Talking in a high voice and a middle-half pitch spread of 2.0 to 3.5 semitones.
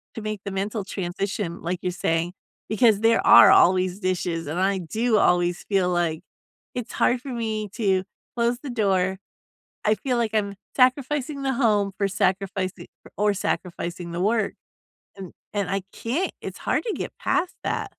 No: high, 200 Hz; average, 4.0 semitones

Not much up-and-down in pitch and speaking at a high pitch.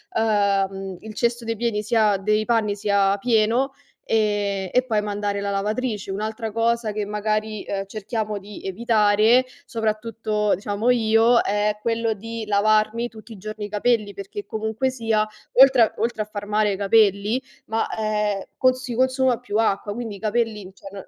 Yes: narrow, 2.0 semitones; high, 215 Hz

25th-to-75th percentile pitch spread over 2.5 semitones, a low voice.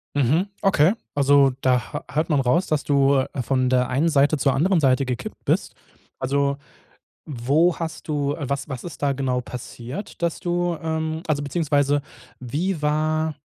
No: average, 2.9 semitones; medium, 145 Hz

